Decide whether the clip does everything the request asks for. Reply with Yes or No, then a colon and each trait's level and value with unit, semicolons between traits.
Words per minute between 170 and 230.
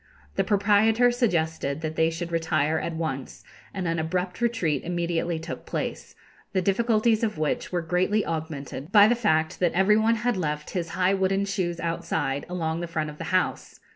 Yes: average, 180 wpm